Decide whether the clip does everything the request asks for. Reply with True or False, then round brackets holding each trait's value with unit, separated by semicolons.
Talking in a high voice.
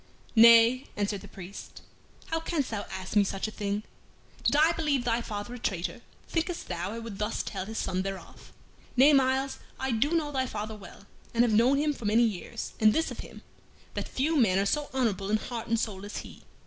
True (225 Hz)